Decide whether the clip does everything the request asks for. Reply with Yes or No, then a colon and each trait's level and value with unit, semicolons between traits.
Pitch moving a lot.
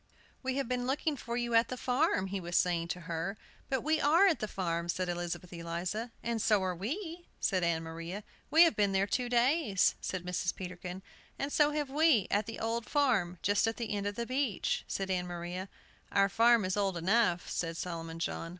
Yes: wide, 5.7 semitones